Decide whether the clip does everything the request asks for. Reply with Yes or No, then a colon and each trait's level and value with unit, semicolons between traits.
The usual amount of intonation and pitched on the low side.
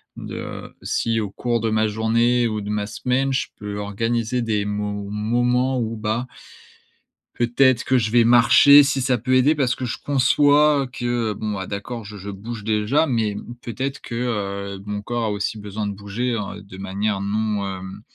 Yes: average, 3.1 semitones; low, 110 Hz